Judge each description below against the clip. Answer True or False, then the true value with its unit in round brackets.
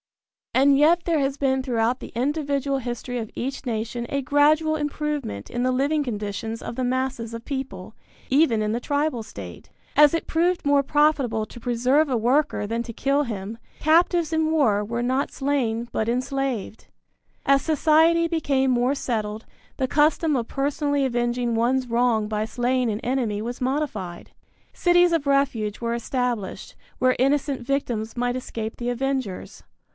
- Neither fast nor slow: True (160 wpm)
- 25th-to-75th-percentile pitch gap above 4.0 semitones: False (3.7 semitones)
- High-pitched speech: True (255 Hz)